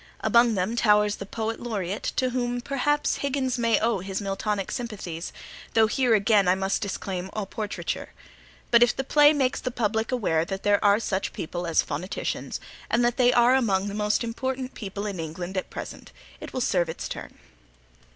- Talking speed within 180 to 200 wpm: Yes, average, 185 wpm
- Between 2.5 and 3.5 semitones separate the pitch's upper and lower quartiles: No, average, 4.0 semitones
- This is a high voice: Yes, high, 215 Hz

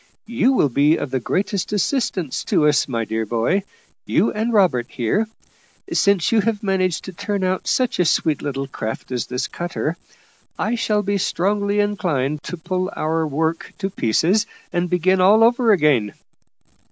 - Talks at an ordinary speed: Yes, average, 165 wpm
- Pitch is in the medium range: Yes, medium, 180 Hz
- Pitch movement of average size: No, wide, 6.1 semitones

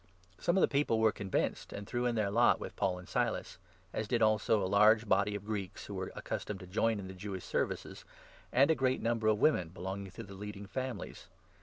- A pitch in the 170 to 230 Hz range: No, low, 105 Hz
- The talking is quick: Yes, fast, 225 wpm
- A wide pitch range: No, average, 2.8 semitones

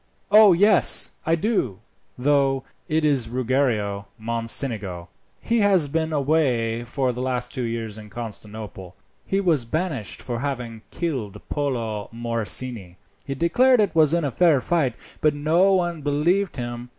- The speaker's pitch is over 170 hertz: No, low, 130 Hz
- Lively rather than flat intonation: Yes, wide, 5.9 semitones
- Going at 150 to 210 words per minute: No, average, 140 wpm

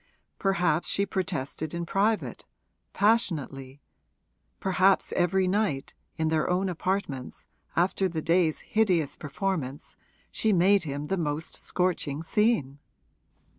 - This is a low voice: No, medium, 175 Hz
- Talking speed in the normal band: No, slow, 110 wpm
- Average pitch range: Yes, average, 4.4 semitones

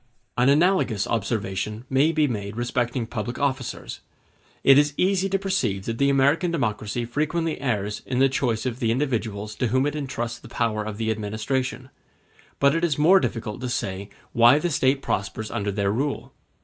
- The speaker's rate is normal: Yes, average, 175 wpm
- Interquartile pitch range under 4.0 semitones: No, average, 4.6 semitones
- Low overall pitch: Yes, low, 125 Hz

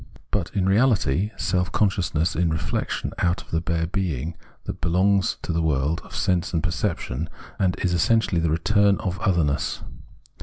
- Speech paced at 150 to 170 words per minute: Yes, average, 165 wpm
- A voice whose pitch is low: Yes, very low, 85 Hz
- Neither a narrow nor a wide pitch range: Yes, average, 3.0 semitones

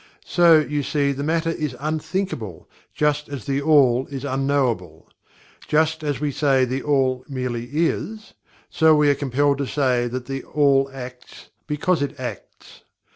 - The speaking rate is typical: Yes, average, 155 wpm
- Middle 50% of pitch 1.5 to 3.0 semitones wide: Yes, average, 2.7 semitones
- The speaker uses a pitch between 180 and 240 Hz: No, medium, 140 Hz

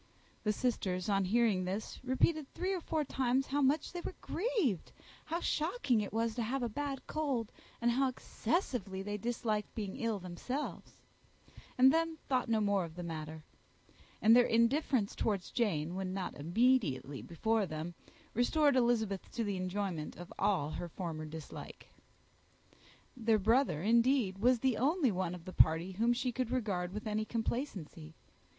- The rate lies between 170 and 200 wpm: No, average, 160 wpm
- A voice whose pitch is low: No, high, 225 Hz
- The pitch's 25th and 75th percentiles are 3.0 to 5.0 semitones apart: No, wide, 5.6 semitones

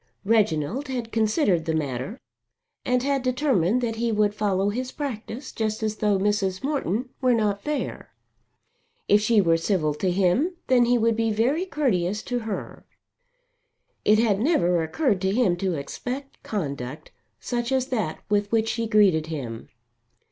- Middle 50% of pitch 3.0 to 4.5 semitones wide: No, average, 5.0 semitones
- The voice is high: Yes, high, 215 Hz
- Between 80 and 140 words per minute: No, average, 155 wpm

